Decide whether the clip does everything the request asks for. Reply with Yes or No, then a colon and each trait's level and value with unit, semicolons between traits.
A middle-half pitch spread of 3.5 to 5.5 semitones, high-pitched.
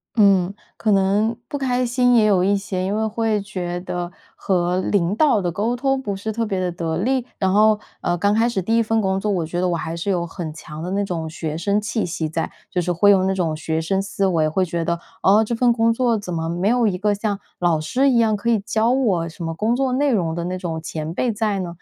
Yes: average, 4.2 semitones; high, 195 Hz